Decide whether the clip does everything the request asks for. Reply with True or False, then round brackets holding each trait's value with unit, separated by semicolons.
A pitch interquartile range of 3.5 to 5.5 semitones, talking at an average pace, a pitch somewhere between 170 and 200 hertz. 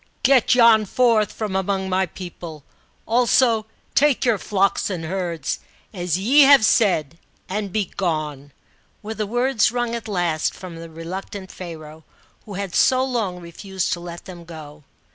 True (4.6 semitones; 160 wpm; 190 Hz)